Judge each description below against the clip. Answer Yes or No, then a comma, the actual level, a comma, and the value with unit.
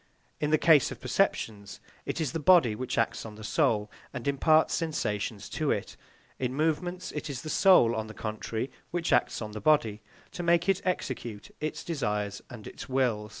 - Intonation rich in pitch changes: Yes, wide, 6.6 semitones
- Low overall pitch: Yes, low, 130 Hz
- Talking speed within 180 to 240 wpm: Yes, average, 190 wpm